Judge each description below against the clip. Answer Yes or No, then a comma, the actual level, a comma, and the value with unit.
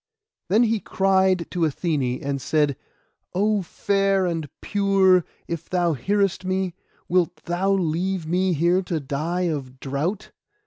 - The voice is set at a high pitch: No, medium, 180 Hz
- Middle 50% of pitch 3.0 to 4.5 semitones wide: Yes, average, 3.3 semitones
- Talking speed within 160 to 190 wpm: No, slow, 135 wpm